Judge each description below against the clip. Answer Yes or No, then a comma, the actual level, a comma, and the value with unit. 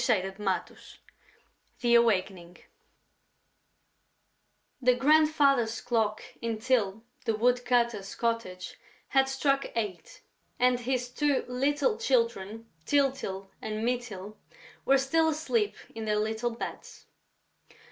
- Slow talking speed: Yes, slow, 100 wpm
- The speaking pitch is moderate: No, high, 235 Hz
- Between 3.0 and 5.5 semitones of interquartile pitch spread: Yes, average, 3.9 semitones